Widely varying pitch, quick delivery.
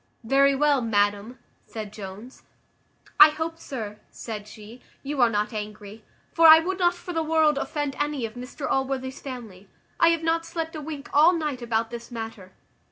No: wide, 5.9 semitones; average, 175 wpm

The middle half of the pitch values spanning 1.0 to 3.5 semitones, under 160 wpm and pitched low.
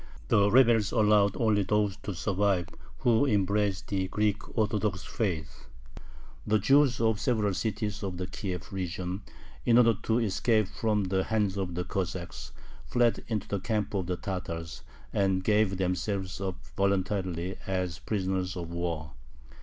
Yes: narrow, 2.6 semitones; average, 145 wpm; low, 100 Hz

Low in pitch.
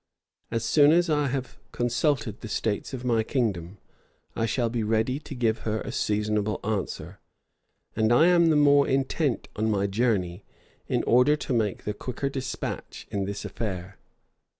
Yes: low, 115 Hz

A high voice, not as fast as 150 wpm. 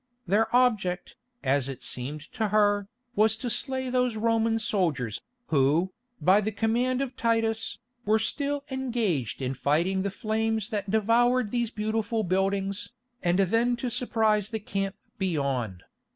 Yes: high, 215 Hz; average, 140 wpm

